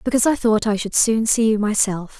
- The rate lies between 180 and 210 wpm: No, fast, 245 wpm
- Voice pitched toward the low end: No, high, 220 Hz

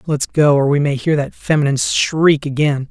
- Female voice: No, male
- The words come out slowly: No, fast, 205 wpm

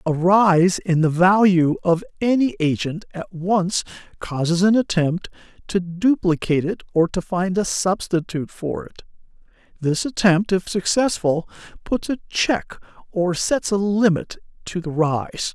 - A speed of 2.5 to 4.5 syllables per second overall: Yes, 4.2 syllables/s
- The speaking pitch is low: No, medium, 185 Hz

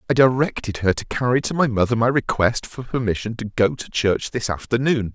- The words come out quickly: Yes, fast, 210 wpm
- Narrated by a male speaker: Yes, male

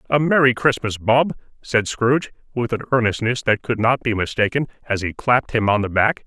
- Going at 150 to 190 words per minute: No, average, 200 wpm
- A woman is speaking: No, male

